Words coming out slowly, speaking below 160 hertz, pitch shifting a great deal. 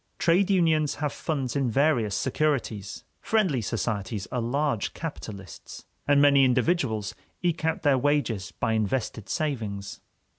Yes: slow, 125 wpm; low, 135 Hz; wide, 5.8 semitones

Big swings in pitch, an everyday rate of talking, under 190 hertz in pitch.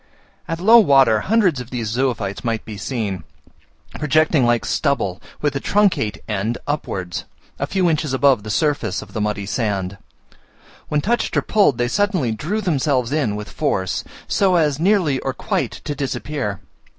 Yes: wide, 6.5 semitones; average, 160 wpm; low, 135 Hz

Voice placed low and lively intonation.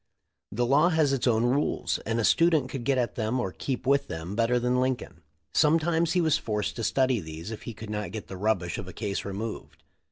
No: low, 120 Hz; average, 4.7 semitones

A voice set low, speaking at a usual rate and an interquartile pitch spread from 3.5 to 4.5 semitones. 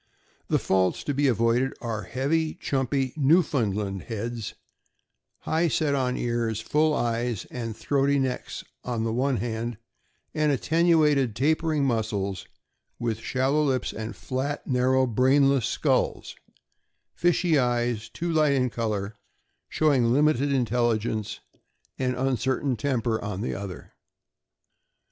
No: low, 125 Hz; slow, 125 wpm; average, 3.8 semitones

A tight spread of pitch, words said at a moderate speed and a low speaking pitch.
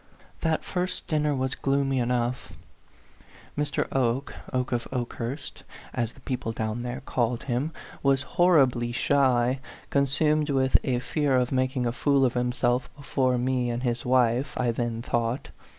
Yes: narrow, 2.3 semitones; average, 150 wpm; low, 130 Hz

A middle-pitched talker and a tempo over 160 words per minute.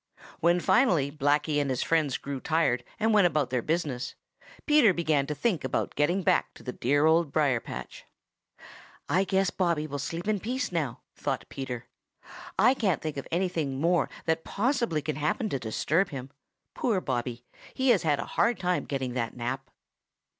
Yes: medium, 155 Hz; average, 175 wpm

